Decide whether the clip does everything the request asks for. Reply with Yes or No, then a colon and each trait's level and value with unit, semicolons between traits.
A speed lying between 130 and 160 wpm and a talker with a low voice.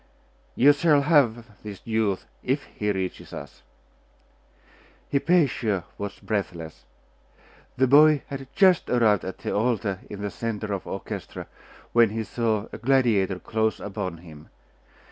Yes: slow, 135 wpm; low, 110 Hz